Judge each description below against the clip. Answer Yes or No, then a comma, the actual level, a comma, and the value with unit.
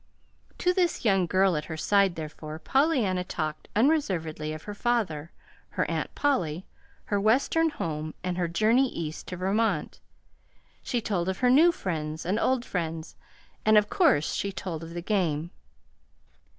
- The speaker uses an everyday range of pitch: No, wide, 6.0 semitones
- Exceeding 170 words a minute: No, average, 150 wpm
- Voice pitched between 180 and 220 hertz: Yes, medium, 185 Hz